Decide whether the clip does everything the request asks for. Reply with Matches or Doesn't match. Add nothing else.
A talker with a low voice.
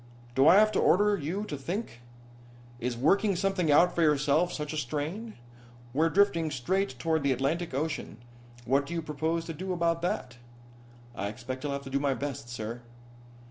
Doesn't match